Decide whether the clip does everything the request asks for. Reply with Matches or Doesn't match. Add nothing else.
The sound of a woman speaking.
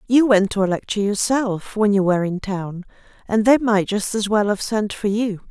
Matches